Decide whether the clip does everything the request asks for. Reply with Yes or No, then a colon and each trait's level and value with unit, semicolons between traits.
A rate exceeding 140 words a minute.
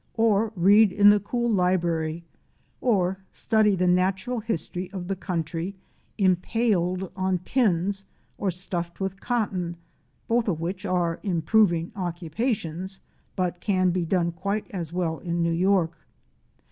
No: slow, 135 wpm